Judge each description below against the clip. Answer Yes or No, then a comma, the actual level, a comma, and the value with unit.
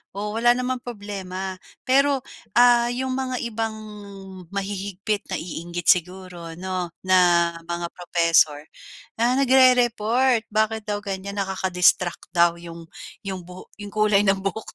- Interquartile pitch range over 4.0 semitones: Yes, average, 4.7 semitones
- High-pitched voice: Yes, high, 200 Hz